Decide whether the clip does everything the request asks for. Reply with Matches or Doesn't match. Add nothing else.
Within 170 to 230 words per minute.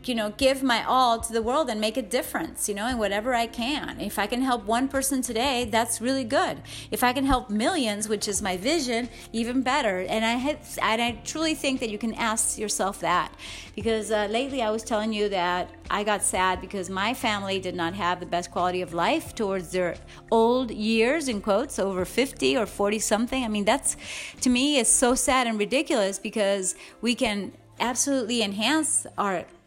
Matches